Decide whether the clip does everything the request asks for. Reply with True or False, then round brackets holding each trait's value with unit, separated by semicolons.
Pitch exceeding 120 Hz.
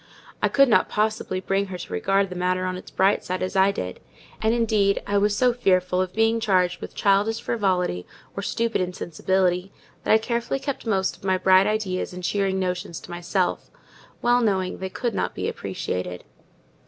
True (190 Hz)